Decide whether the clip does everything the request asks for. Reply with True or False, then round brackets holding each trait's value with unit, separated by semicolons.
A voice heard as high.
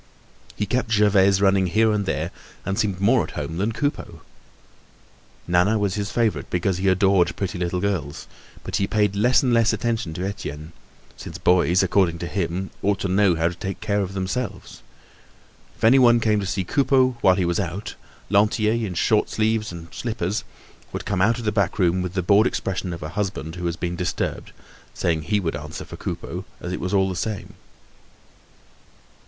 False (95 Hz)